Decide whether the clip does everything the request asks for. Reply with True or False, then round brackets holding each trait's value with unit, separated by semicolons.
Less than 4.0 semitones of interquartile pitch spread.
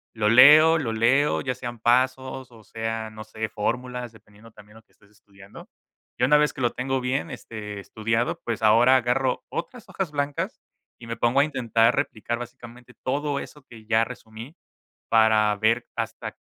True (2.9 semitones)